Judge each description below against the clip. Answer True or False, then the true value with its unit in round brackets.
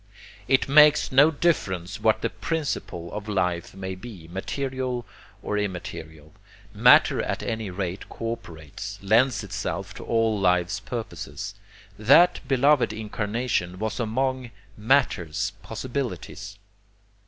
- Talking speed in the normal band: False (115 wpm)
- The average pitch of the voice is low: True (110 Hz)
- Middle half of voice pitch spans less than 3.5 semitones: False (5.5 semitones)